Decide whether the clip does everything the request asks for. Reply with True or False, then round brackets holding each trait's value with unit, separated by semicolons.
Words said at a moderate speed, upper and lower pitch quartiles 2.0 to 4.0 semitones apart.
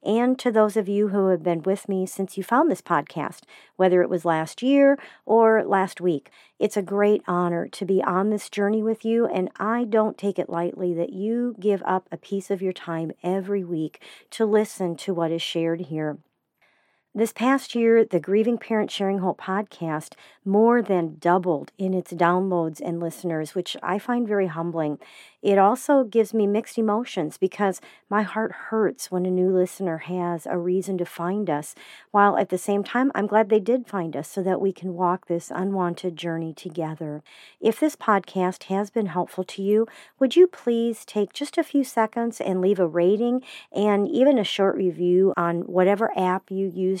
True (190 wpm; 3.6 semitones)